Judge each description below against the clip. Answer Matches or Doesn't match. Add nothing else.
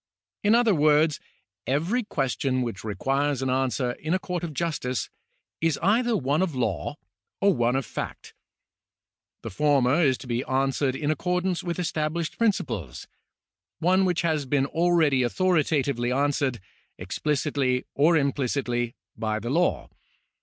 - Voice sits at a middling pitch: Matches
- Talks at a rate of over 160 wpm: Doesn't match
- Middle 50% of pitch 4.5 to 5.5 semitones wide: Matches